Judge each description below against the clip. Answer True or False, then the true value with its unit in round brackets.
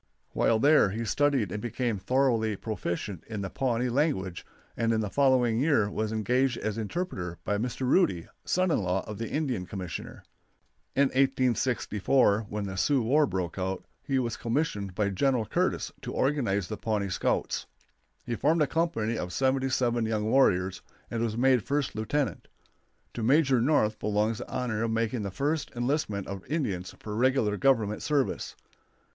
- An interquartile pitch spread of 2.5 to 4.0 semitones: False (4.5 semitones)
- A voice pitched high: False (115 Hz)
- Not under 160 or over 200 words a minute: True (165 wpm)